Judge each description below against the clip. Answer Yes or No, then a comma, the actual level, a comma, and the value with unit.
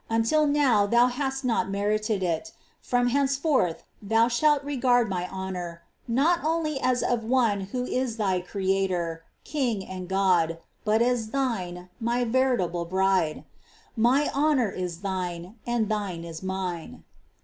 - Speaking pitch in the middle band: No, high, 220 Hz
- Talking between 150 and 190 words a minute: No, average, 140 wpm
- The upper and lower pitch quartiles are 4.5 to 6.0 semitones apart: Yes, average, 5.3 semitones